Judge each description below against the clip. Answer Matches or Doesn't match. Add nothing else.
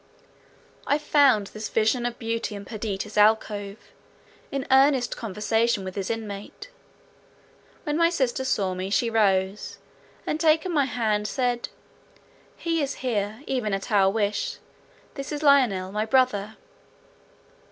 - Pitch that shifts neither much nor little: Matches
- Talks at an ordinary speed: Doesn't match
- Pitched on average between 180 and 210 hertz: Doesn't match